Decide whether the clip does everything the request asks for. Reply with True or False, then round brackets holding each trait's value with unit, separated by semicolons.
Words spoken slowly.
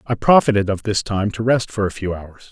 False (265 wpm)